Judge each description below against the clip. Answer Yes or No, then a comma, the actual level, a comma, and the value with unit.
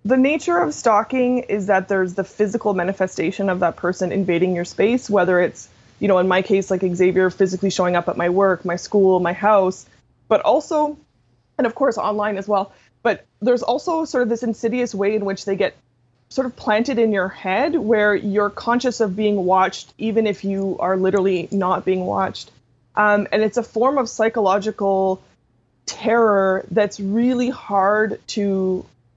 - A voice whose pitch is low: No, high, 200 Hz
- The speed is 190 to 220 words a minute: No, average, 180 wpm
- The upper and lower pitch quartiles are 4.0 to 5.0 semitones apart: No, average, 3.4 semitones